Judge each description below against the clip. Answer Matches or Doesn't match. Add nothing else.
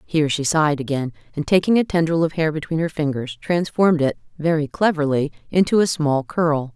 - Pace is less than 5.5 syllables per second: Doesn't match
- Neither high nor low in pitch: Matches